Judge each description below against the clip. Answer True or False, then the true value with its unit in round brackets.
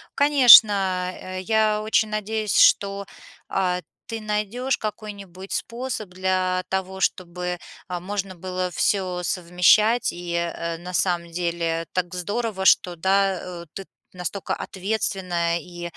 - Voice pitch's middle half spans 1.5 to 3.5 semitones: True (2.9 semitones)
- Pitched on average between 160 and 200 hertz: True (185 Hz)